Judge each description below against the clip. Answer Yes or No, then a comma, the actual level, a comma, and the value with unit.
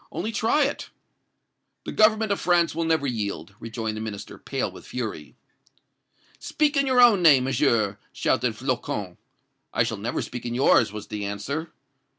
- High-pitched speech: No, low, 130 Hz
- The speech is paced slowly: No, average, 165 wpm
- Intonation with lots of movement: Yes, wide, 8.9 semitones